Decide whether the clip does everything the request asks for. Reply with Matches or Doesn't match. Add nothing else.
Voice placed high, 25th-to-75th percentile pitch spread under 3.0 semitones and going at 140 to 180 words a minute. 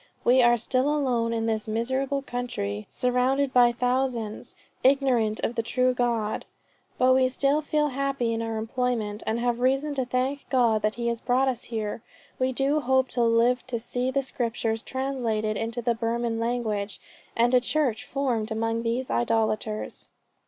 Matches